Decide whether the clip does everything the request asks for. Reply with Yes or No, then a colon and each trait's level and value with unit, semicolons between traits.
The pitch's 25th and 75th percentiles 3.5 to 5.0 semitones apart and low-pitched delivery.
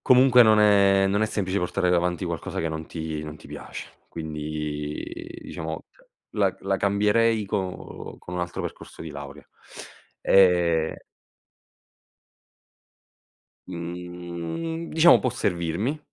Yes: average, 4.4 semitones; very low, 90 Hz